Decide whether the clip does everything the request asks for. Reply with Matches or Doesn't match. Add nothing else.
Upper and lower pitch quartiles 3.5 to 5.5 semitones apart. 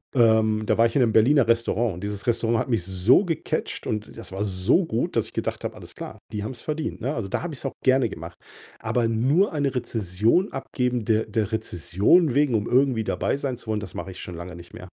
Matches